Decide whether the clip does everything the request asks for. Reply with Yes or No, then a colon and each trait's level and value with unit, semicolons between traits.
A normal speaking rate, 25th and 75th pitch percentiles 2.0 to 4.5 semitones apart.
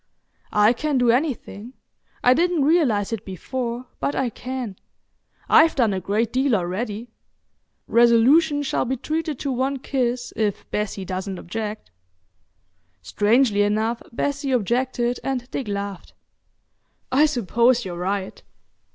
No: slow, 125 wpm; average, 4.2 semitones